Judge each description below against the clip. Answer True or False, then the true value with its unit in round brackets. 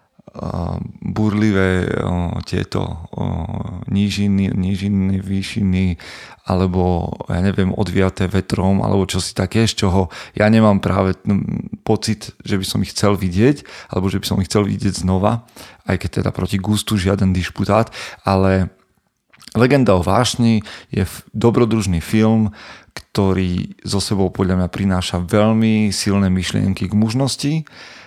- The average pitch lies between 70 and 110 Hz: True (100 Hz)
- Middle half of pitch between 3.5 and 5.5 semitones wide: False (2.4 semitones)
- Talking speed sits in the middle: True (135 wpm)